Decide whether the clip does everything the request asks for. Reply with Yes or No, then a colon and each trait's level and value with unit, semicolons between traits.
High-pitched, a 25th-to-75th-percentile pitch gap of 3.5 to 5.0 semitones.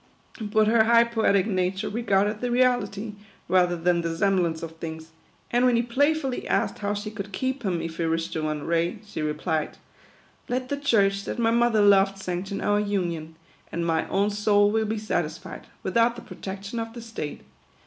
Yes: high, 200 Hz; average, 4.6 semitones